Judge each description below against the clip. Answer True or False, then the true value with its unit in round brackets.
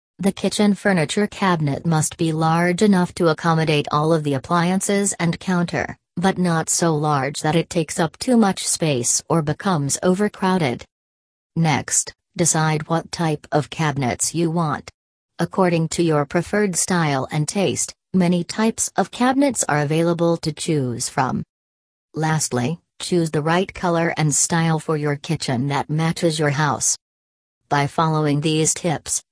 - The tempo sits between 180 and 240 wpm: False (145 wpm)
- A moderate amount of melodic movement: True (3.1 semitones)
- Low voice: False (165 Hz)